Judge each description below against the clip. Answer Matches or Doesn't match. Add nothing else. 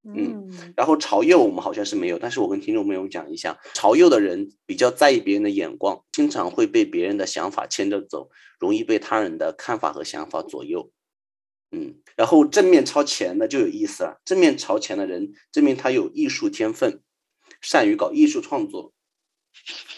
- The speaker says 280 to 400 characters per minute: Matches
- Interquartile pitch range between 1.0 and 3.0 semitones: Matches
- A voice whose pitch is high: Matches